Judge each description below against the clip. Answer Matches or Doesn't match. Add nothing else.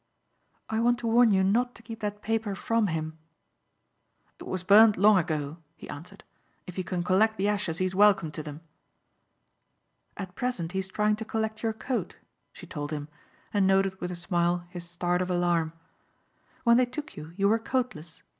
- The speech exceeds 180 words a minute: Matches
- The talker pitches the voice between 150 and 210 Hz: Matches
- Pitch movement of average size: Matches